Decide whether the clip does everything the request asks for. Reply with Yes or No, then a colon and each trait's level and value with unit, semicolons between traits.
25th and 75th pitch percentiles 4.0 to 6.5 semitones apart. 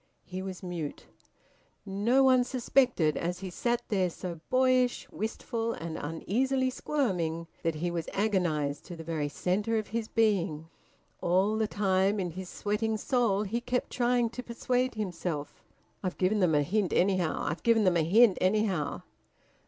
Yes: average, 5.0 semitones